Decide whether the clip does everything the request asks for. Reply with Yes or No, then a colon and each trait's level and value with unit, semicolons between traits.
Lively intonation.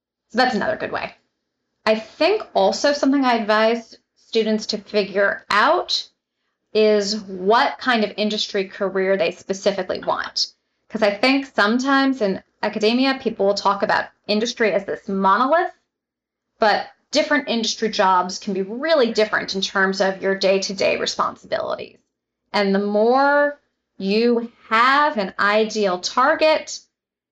No: average, 4.1 semitones